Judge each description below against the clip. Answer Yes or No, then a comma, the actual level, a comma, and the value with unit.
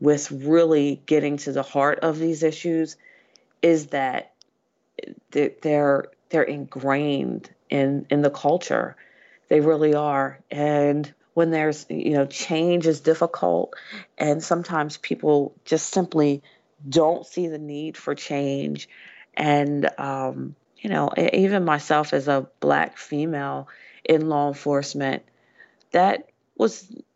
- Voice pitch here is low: No, medium, 150 Hz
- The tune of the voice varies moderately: No, narrow, 2.1 semitones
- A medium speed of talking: No, slow, 120 wpm